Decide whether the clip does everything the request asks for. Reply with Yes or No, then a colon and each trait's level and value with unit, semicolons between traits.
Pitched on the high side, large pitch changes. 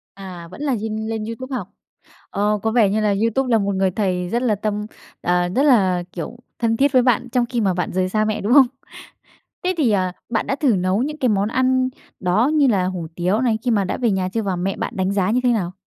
No: high, 215 Hz; average, 4.6 semitones